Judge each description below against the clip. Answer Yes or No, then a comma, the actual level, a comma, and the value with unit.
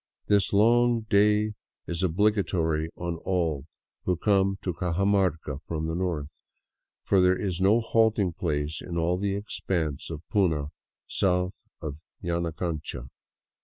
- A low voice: Yes, very low, 90 Hz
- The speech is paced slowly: Yes, slow, 130 wpm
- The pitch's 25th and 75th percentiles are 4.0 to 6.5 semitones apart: No, average, 3.6 semitones